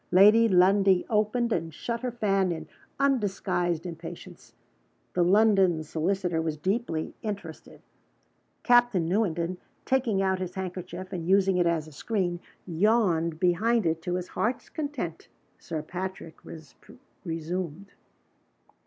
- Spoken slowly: Yes, slow, 125 wpm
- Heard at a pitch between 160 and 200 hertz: Yes, medium, 185 Hz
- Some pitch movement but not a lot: Yes, average, 4.0 semitones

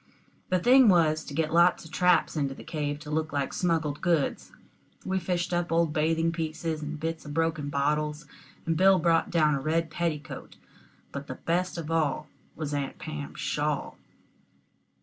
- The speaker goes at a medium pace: Yes, average, 170 wpm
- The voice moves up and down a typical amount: No, narrow, 2.1 semitones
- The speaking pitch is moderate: Yes, medium, 160 Hz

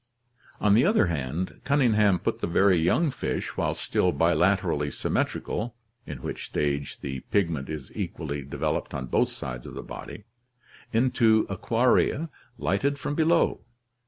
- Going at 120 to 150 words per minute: Yes, average, 140 wpm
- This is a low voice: Yes, very low, 95 Hz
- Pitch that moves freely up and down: Yes, wide, 8.2 semitones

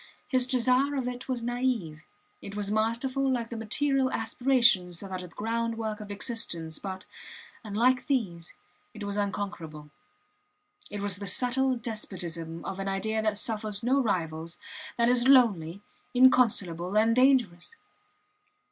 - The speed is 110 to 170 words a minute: Yes, average, 140 wpm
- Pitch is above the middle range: Yes, high, 220 Hz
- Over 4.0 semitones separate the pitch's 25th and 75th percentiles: Yes, average, 4.6 semitones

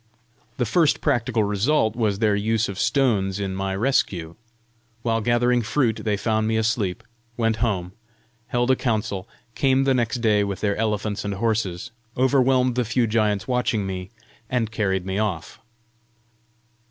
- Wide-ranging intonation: No, average, 3.2 semitones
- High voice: No, low, 110 Hz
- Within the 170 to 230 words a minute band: No, average, 155 wpm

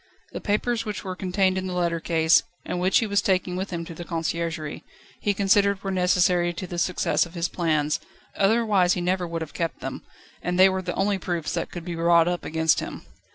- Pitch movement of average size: No, narrow, 2.2 semitones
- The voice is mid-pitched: Yes, medium, 180 Hz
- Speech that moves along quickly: Yes, fast, 220 wpm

